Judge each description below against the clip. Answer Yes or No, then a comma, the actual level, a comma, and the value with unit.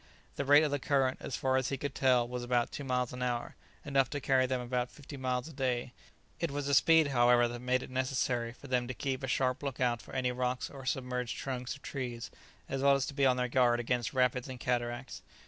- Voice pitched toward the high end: No, low, 130 Hz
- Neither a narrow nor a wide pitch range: No, narrow, 1.6 semitones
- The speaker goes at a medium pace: No, fast, 245 wpm